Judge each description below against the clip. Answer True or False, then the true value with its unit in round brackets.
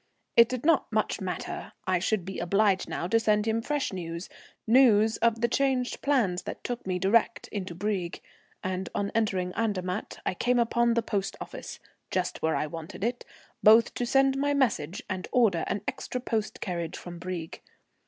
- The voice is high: True (210 Hz)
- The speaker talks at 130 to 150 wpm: False (180 wpm)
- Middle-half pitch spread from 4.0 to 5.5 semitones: True (4.4 semitones)